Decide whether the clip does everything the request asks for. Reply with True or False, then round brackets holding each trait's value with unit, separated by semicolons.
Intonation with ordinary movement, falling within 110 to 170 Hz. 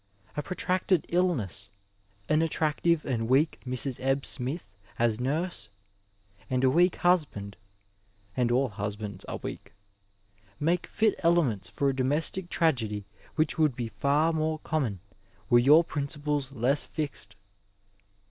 False (6.2 semitones; 135 Hz)